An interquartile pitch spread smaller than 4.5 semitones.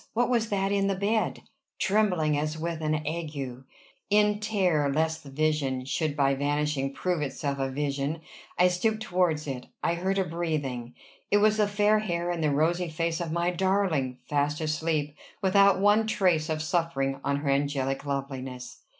No: average, 5.0 semitones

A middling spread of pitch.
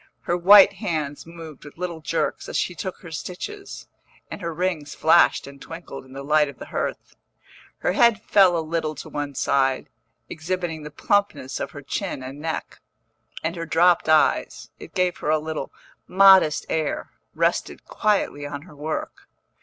Yes: average, 3.5 semitones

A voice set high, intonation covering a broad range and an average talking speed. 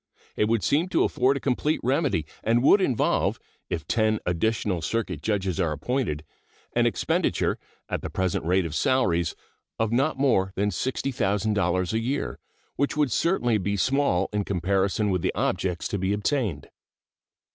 No: low, 105 Hz; wide, 5.7 semitones; average, 155 wpm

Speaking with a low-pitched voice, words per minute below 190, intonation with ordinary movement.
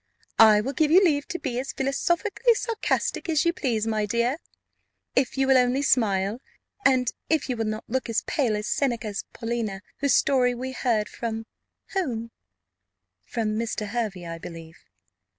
No: high, 240 Hz; average, 165 wpm; average, 4.1 semitones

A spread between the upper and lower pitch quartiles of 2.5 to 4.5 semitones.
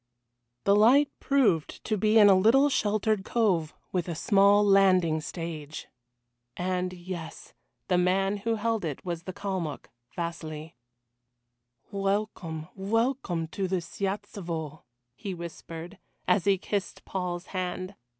Yes: average, 3.3 semitones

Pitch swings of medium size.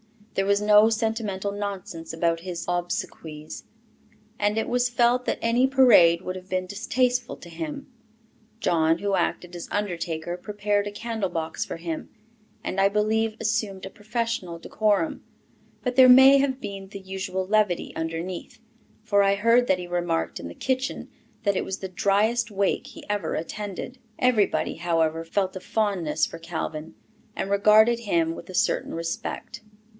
Yes: average, 4.2 semitones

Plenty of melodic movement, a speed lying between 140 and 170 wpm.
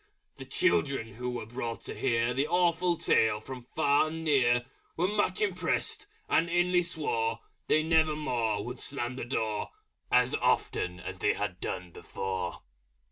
Yes: wide, 6.6 semitones; average, 150 wpm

